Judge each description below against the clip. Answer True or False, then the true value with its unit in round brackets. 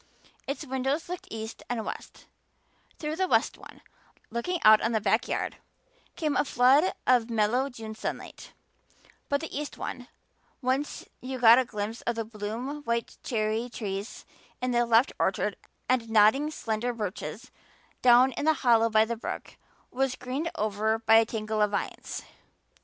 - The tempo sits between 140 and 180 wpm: True (160 wpm)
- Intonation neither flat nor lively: True (3.3 semitones)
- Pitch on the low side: False (235 Hz)